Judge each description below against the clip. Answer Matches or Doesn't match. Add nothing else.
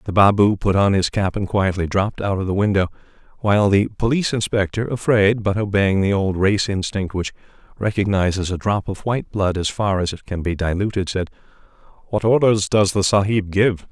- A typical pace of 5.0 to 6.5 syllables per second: Matches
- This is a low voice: Matches